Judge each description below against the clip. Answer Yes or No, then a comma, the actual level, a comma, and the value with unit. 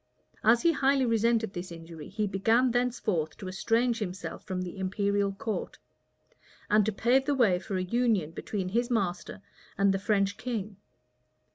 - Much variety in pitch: No, average, 3.9 semitones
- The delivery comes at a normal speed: Yes, average, 160 wpm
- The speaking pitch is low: No, high, 205 Hz